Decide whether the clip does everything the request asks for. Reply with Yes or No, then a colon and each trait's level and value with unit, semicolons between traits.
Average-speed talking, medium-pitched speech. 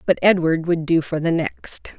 No: fast, 210 wpm; medium, 165 Hz